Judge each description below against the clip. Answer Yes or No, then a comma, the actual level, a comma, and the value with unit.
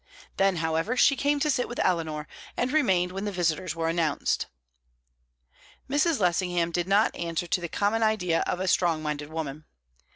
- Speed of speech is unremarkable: Yes, average, 170 wpm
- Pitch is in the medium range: Yes, medium, 180 Hz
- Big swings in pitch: No, average, 4.5 semitones